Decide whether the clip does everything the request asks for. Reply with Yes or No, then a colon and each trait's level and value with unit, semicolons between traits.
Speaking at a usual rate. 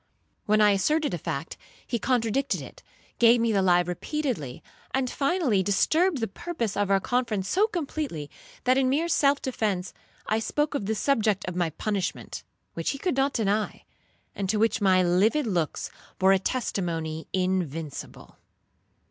Yes: average, 160 wpm